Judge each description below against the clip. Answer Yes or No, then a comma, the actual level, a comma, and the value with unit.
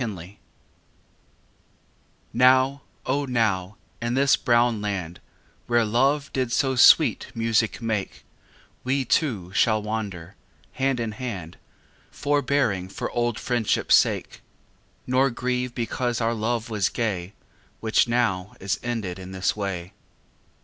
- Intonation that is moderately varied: Yes, average, 4.2 semitones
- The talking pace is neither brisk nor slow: No, slow, 120 wpm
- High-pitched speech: No, low, 115 Hz